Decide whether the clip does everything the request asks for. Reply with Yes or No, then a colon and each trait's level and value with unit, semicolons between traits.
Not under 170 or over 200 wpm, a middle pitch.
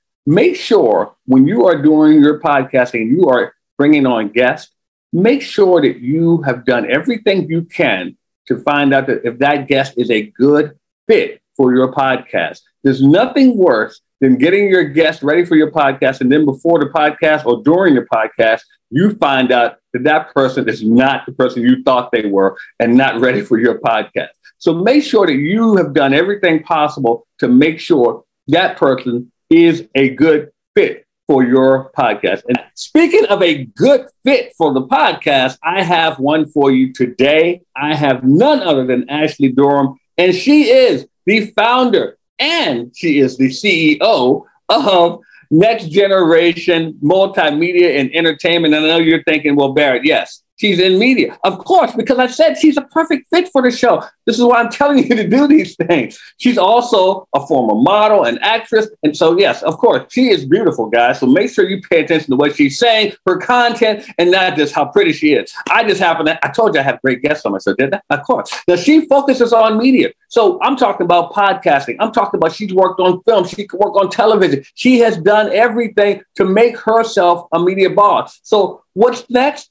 Yes: average, 195 wpm; medium, 175 Hz